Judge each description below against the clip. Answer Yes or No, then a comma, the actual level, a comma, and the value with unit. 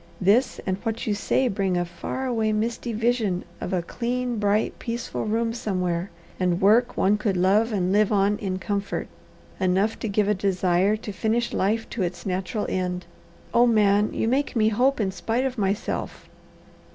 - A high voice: Yes, high, 210 Hz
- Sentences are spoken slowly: No, average, 175 wpm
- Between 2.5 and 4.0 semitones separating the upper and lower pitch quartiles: Yes, average, 3.3 semitones